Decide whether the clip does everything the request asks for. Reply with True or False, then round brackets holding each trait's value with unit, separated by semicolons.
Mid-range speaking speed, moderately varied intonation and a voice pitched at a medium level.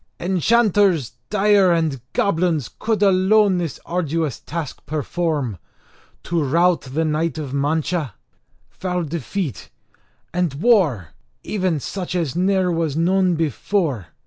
False (115 wpm; 3.7 semitones; 170 Hz)